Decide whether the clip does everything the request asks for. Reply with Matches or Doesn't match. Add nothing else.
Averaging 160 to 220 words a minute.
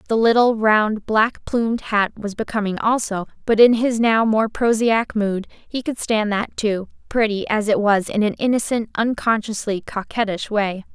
Matches